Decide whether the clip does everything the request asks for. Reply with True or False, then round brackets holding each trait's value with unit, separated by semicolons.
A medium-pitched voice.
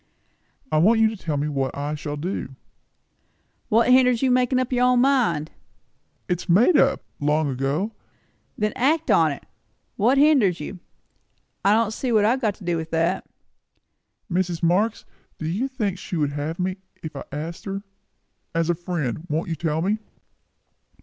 True (180 Hz)